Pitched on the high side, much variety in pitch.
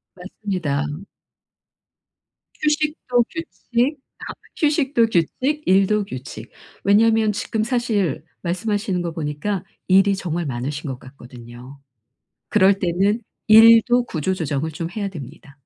Yes: high, 195 Hz; wide, 6.8 semitones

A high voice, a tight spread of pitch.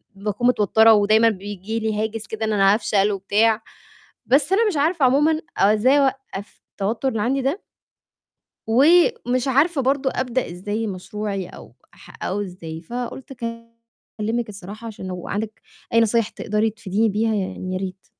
No: high, 220 Hz; average, 3.7 semitones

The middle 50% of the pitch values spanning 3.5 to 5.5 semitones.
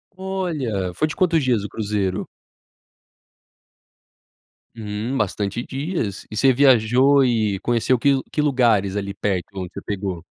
Yes: average, 5.2 semitones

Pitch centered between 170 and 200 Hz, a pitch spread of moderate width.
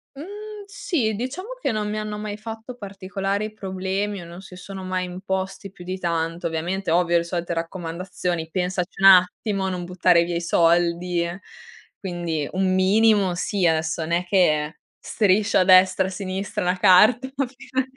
Yes: medium, 185 Hz; average, 3.0 semitones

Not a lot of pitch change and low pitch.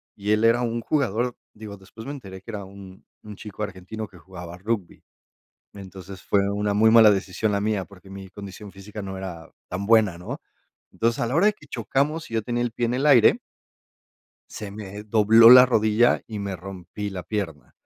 No: average, 3.0 semitones; low, 105 Hz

